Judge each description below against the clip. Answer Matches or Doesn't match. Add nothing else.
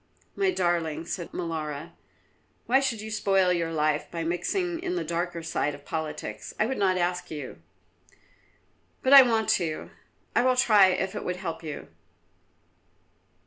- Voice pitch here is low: Doesn't match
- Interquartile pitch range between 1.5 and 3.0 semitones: Doesn't match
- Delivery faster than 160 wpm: Doesn't match